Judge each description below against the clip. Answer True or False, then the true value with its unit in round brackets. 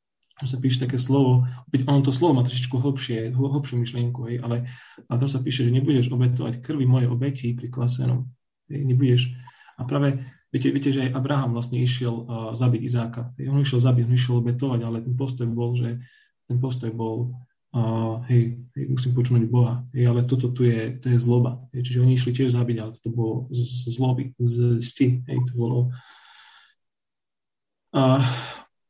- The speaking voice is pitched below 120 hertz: False (125 Hz)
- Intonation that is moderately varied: False (1.4 semitones)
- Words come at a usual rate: False (175 wpm)